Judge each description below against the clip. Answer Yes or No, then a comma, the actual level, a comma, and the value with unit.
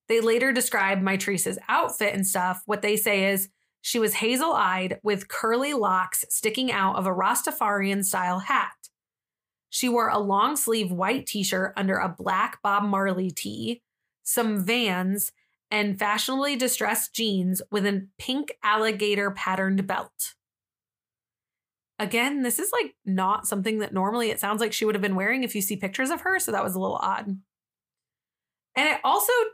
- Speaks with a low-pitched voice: No, high, 205 Hz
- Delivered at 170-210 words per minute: No, average, 155 wpm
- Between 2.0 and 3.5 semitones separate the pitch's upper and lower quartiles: Yes, average, 3.2 semitones